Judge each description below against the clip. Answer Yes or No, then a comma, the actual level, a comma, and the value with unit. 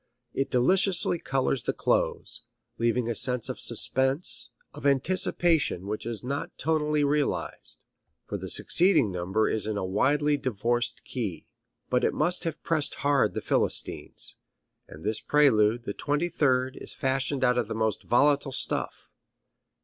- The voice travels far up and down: No, average, 4.4 semitones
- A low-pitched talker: Yes, low, 130 Hz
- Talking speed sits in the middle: Yes, average, 150 wpm